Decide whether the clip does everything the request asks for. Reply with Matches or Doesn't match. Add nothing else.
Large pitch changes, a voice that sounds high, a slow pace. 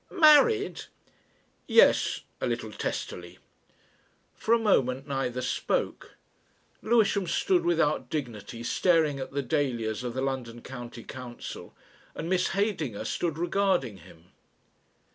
Doesn't match